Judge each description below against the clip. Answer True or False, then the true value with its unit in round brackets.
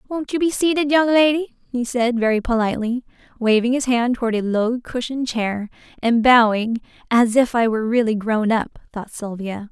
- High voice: True (240 Hz)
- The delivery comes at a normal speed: True (180 wpm)